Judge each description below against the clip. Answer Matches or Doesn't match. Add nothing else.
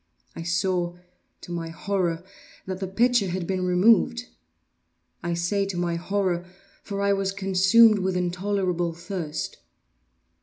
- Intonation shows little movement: Matches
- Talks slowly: Matches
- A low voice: Doesn't match